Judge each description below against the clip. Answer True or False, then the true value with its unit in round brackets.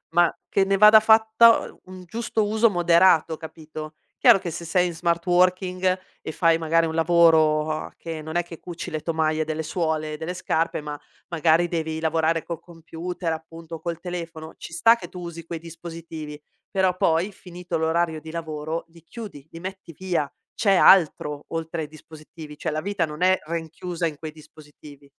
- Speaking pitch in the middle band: True (165 Hz)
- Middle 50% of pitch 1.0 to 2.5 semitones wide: True (2.1 semitones)